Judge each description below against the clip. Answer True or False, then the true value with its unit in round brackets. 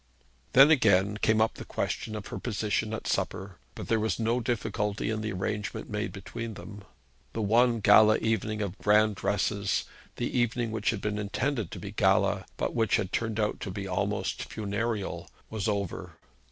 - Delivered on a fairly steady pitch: True (2.0 semitones)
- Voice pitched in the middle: False (105 Hz)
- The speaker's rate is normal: True (180 wpm)